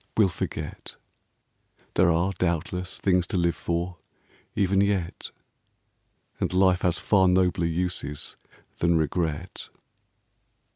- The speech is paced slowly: Yes, slow, 110 wpm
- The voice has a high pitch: No, very low, 90 Hz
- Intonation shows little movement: Yes, narrow, 1.7 semitones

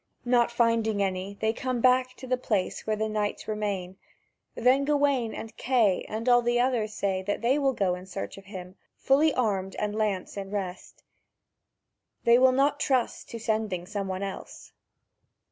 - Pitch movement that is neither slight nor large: Yes, average, 4.1 semitones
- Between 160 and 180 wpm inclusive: Yes, average, 175 wpm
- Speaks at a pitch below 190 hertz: No, high, 220 Hz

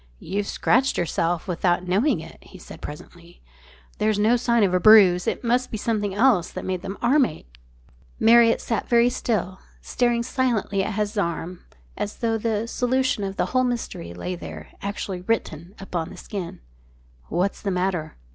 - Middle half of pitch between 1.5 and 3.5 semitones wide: No, average, 4.7 semitones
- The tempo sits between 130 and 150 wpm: No, average, 170 wpm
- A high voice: Yes, high, 200 Hz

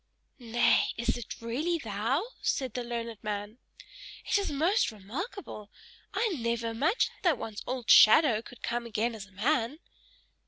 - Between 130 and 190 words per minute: Yes, average, 150 wpm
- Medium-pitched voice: No, high, 235 Hz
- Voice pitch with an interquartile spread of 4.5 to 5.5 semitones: Yes, average, 4.8 semitones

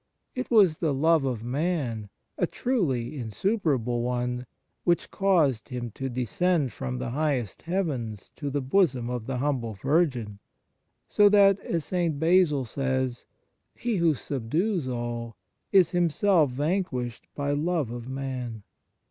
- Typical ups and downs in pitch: No, wide, 5.9 semitones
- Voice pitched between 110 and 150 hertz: Yes, low, 135 Hz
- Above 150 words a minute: No, slow, 135 wpm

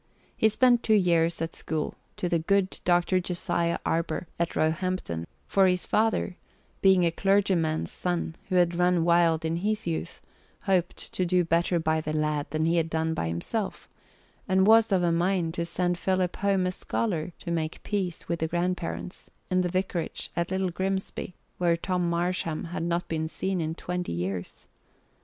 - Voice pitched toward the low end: No, medium, 175 Hz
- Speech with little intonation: Yes, narrow, 2.2 semitones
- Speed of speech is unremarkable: Yes, average, 175 wpm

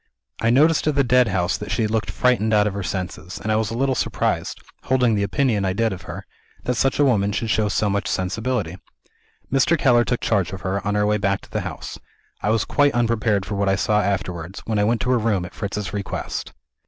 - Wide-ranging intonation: No, average, 3.4 semitones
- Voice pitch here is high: No, low, 105 Hz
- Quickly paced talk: Yes, fast, 235 wpm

